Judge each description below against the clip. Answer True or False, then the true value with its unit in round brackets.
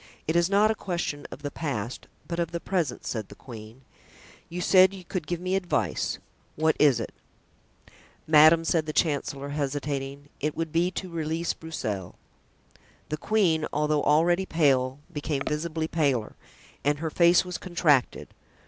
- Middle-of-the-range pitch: True (155 Hz)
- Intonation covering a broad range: False (3.3 semitones)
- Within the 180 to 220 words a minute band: False (155 wpm)